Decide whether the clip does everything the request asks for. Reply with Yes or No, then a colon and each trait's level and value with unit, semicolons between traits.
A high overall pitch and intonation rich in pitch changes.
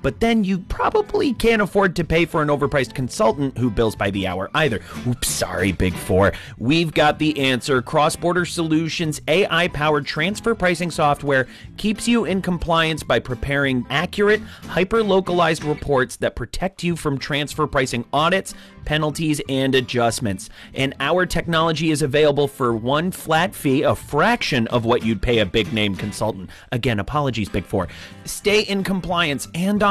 No: medium, 150 Hz; wide, 6.2 semitones